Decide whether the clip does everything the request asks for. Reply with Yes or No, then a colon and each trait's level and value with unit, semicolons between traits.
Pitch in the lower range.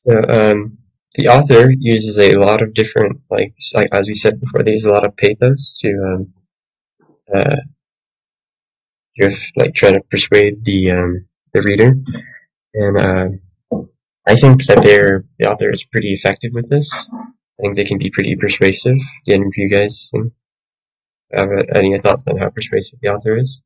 Yes: low, 105 Hz